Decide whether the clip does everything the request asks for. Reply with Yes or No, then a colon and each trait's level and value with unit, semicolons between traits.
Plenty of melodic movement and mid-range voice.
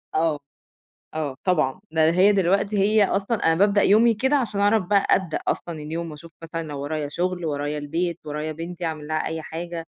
No: average, 4.1 semitones; medium, 170 Hz